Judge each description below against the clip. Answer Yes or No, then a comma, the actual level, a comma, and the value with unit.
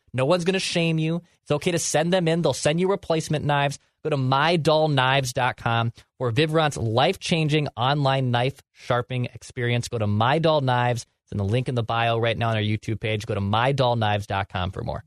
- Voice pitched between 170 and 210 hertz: No, low, 130 Hz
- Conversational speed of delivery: Yes, average, 195 wpm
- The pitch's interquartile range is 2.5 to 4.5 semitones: No, average, 5.0 semitones